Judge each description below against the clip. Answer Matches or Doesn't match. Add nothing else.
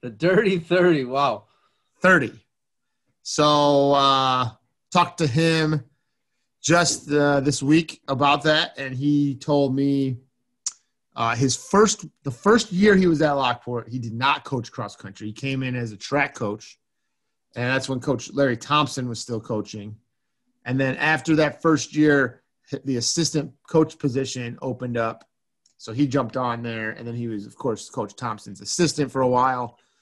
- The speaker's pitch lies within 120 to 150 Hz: Matches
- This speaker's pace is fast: Doesn't match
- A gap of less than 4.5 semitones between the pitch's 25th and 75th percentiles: Matches